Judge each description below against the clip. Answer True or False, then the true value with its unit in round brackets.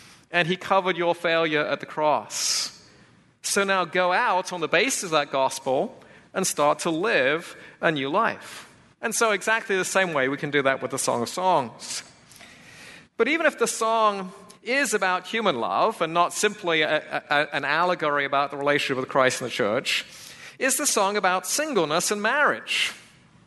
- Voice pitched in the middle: True (180 Hz)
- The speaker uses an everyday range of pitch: False (6.0 semitones)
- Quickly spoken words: False (180 wpm)